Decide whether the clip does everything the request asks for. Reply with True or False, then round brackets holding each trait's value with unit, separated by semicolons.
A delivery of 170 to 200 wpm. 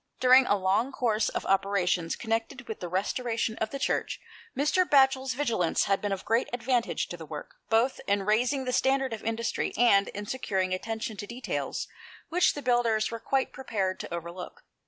True (180 wpm)